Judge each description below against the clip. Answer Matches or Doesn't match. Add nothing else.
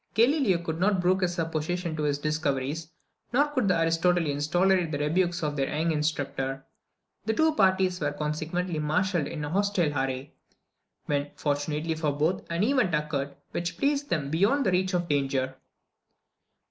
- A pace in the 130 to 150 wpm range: Doesn't match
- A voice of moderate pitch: Matches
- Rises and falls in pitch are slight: Doesn't match